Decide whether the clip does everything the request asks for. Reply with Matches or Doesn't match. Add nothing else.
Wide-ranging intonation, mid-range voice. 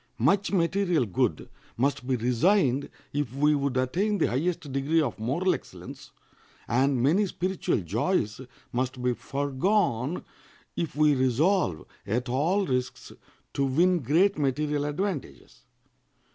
Matches